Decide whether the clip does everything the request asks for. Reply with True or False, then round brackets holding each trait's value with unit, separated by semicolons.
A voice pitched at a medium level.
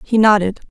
False (205 Hz)